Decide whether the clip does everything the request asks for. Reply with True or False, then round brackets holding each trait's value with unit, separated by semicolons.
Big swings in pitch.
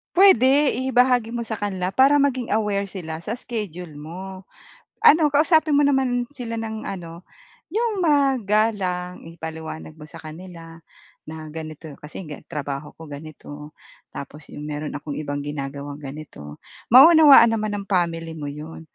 True (7.9 semitones)